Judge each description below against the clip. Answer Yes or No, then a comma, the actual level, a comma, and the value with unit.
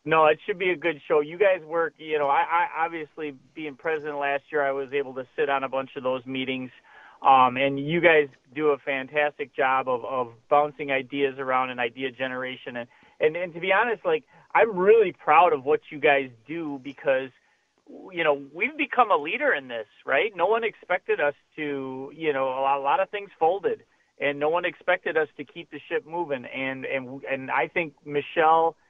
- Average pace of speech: No, fast, 210 wpm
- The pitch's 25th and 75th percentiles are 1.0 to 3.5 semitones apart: No, average, 3.9 semitones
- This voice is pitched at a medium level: Yes, medium, 145 Hz